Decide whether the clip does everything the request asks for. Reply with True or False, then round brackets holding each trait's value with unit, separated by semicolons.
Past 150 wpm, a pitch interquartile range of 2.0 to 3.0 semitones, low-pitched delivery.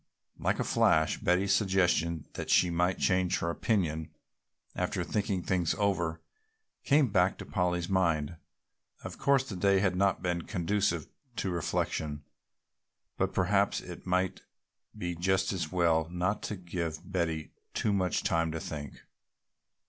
False (140 wpm; 2.4 semitones; 90 Hz)